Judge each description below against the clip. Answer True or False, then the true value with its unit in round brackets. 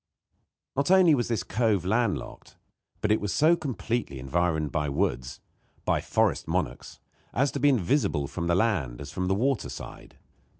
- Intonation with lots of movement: True (8.6 semitones)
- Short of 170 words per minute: False (175 wpm)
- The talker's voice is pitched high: False (105 Hz)